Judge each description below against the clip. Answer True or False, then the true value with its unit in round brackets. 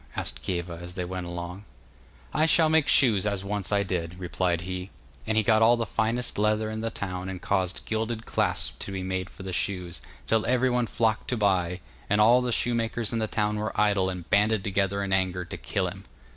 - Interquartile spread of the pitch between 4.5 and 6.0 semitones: False (3.3 semitones)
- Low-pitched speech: True (100 Hz)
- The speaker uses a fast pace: True (215 wpm)